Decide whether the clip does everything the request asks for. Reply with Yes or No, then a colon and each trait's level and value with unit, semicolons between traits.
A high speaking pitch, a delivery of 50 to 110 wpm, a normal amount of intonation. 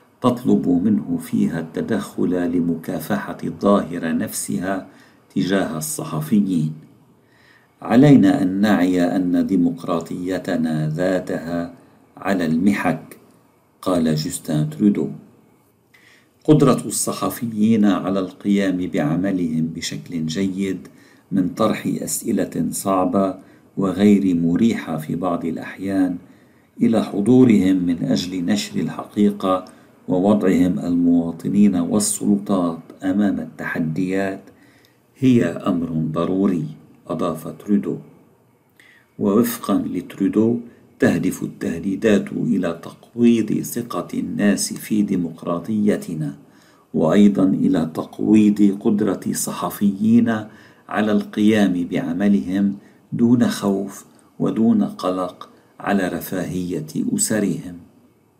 No: very low, 95 Hz; average, 80 wpm; average, 3.5 semitones